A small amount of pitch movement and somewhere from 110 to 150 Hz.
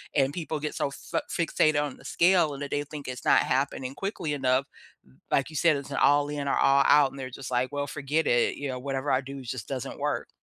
Yes: narrow, 1.8 semitones; medium, 140 Hz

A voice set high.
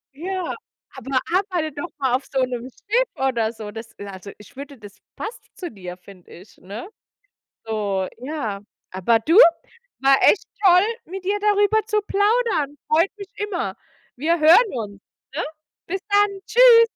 Yes: very high, 290 Hz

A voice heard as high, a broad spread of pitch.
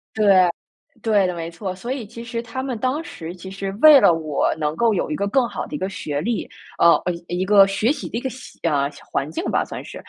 Yes: high, 200 Hz; wide, 5.8 semitones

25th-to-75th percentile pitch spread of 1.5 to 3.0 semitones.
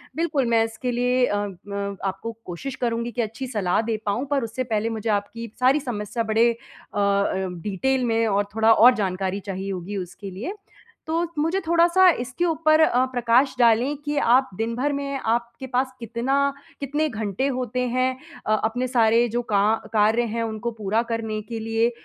No: average, 3.4 semitones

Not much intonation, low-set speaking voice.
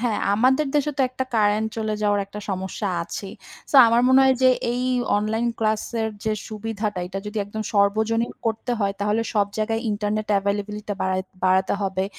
No: narrow, 1.9 semitones; high, 215 Hz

